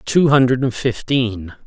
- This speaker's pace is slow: Yes, slow, 110 wpm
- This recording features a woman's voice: No, male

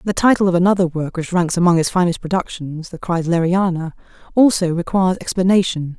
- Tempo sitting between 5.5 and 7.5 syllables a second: Yes, 5.9 syllables/s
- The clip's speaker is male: No, female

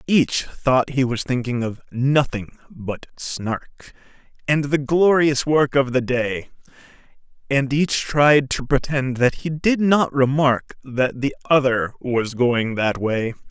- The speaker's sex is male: Yes, male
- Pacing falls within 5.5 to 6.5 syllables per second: No, 3.5 syllables/s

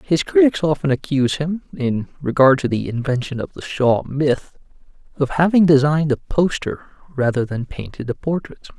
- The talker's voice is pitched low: No, medium, 145 Hz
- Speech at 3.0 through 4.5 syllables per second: No, 5.1 syllables/s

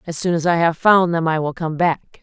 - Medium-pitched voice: Yes, medium, 165 Hz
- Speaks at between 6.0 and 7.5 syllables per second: No, 5.3 syllables/s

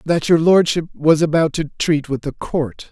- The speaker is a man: Yes, male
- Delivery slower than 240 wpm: Yes, fast, 205 wpm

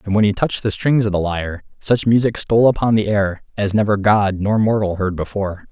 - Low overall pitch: Yes, low, 105 Hz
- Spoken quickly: Yes, fast, 230 wpm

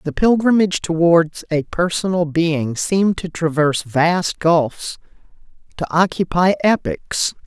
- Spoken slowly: Yes, slow, 115 wpm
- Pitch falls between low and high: Yes, medium, 170 Hz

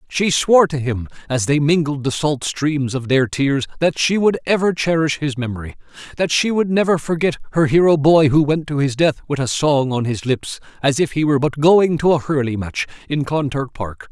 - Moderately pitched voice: Yes, medium, 145 Hz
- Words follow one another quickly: Yes, fast, 220 wpm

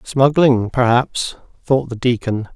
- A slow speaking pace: Yes, slow, 115 wpm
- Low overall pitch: Yes, low, 125 Hz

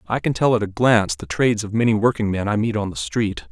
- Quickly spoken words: Yes, fast, 275 wpm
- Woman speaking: No, male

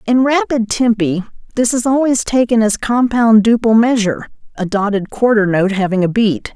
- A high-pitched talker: Yes, high, 225 Hz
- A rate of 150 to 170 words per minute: Yes, average, 165 wpm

